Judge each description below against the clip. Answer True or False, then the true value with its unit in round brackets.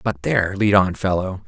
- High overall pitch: False (100 Hz)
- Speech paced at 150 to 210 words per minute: True (205 wpm)